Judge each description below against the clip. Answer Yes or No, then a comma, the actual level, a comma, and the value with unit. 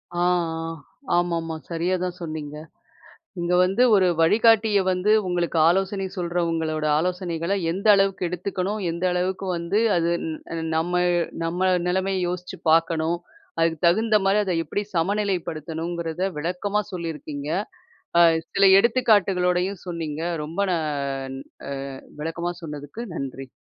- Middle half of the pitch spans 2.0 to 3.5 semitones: Yes, average, 2.8 semitones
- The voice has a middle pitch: Yes, medium, 175 Hz